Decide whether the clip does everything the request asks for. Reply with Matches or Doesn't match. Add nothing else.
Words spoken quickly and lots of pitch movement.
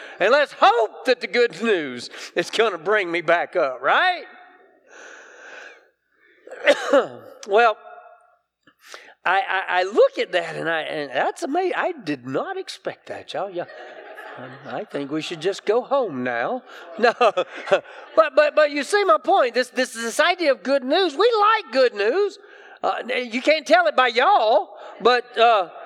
Doesn't match